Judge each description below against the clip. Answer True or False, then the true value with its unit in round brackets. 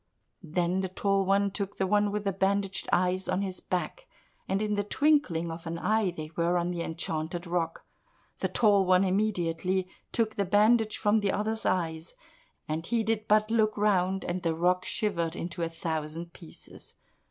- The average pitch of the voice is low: False (185 Hz)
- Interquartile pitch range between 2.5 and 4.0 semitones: True (3.4 semitones)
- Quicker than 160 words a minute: True (175 wpm)